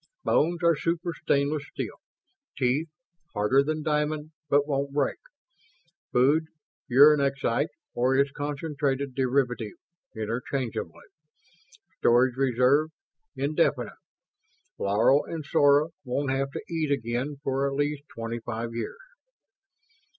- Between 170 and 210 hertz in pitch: No, medium, 140 Hz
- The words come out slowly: Yes, slow, 105 wpm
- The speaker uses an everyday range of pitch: Yes, average, 3.0 semitones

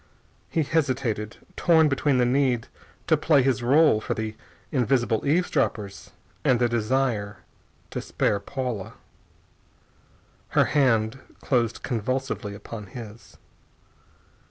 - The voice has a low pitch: Yes, low, 125 Hz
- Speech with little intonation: No, average, 3.8 semitones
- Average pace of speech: No, slow, 110 wpm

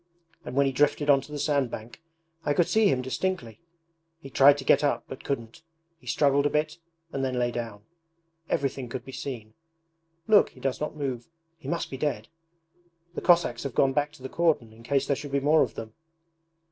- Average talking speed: No, fast, 210 wpm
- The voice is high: No, medium, 140 Hz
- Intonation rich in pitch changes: No, average, 2.8 semitones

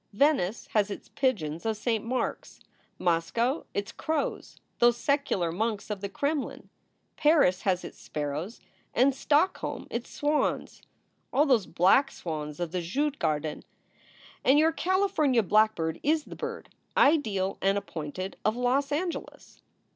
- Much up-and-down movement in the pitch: Yes, wide, 7.7 semitones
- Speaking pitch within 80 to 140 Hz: No, high, 225 Hz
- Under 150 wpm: Yes, average, 140 wpm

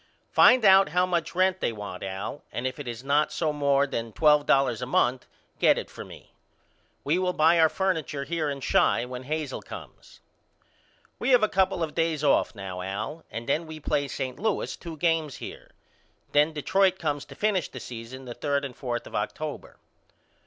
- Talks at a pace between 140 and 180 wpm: No, average, 195 wpm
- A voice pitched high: No, medium, 150 Hz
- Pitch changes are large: No, average, 4.8 semitones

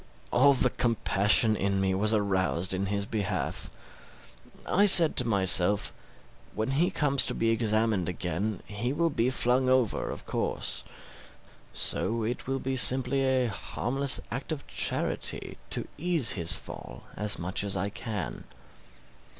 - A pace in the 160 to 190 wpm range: No, average, 145 wpm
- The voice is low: Yes, low, 115 Hz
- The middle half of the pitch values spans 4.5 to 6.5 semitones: Yes, average, 4.8 semitones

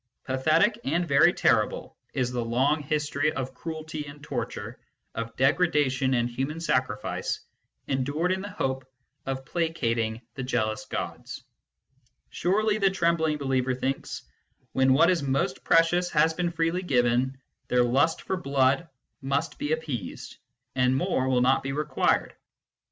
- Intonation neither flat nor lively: Yes, average, 4.0 semitones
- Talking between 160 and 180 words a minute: No, average, 140 wpm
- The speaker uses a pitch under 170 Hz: Yes, medium, 140 Hz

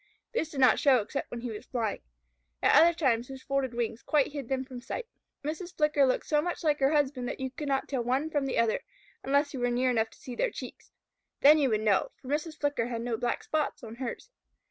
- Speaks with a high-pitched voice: Yes, very high, 265 Hz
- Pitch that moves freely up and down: No, average, 3.5 semitones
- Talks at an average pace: No, fast, 240 wpm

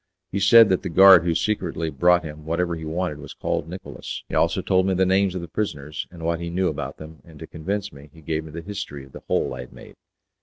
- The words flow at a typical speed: No, fast, 260 wpm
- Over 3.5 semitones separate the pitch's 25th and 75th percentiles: No, average, 3.1 semitones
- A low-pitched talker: Yes, very low, 85 Hz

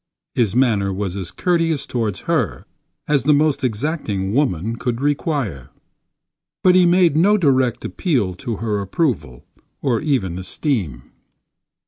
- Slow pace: Yes, slow, 130 wpm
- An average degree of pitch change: No, wide, 7.4 semitones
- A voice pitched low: Yes, low, 125 Hz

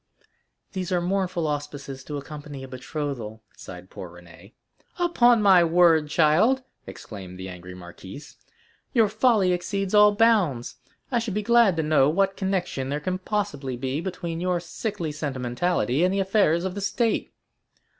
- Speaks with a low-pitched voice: No, medium, 170 Hz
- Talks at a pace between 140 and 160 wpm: Yes, average, 155 wpm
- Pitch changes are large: Yes, wide, 6.5 semitones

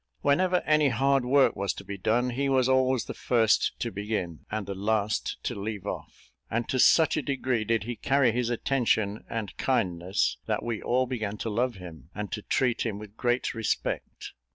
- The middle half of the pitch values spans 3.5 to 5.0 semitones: Yes, average, 3.9 semitones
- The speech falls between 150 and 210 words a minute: Yes, average, 195 wpm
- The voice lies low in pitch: Yes, low, 115 Hz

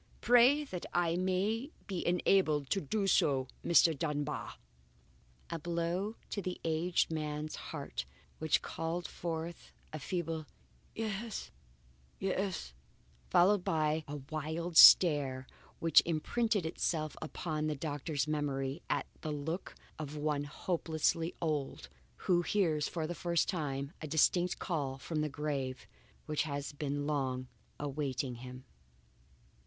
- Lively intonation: No, average, 3.2 semitones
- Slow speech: Yes, slow, 125 wpm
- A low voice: No, medium, 155 Hz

